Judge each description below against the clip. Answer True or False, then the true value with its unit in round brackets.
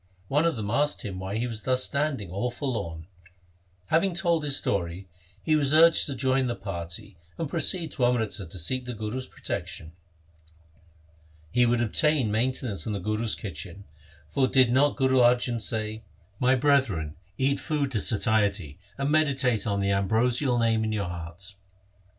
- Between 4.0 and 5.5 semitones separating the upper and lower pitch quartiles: True (5.2 semitones)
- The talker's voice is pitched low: True (120 Hz)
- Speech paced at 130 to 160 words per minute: False (175 wpm)